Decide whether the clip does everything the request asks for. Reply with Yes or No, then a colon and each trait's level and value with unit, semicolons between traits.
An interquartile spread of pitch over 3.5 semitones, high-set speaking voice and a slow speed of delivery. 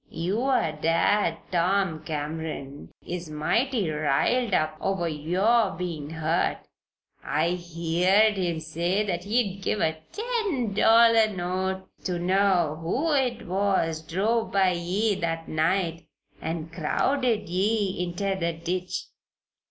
No: average, 4.1 semitones; medium, 180 Hz; slow, 120 wpm